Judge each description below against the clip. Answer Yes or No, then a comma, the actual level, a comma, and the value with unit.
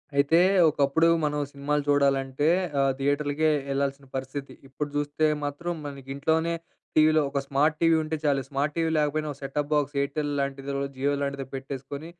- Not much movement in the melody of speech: Yes, narrow, 1.7 semitones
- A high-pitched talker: No, medium, 145 Hz